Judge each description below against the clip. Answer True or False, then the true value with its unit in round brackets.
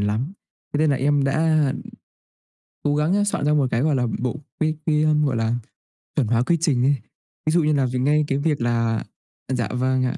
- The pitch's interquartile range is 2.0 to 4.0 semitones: True (3.6 semitones)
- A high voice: False (140 Hz)